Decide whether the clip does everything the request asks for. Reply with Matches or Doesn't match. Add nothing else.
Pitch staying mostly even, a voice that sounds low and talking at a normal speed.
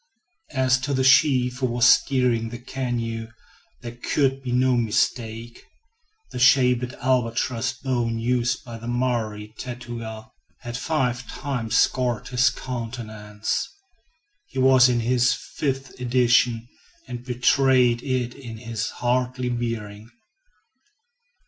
Doesn't match